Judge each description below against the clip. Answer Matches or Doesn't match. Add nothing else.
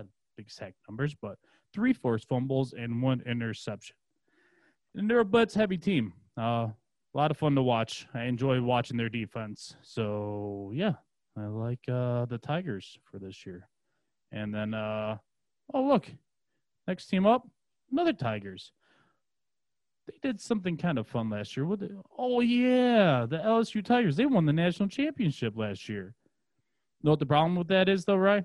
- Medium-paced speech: Matches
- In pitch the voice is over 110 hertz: Matches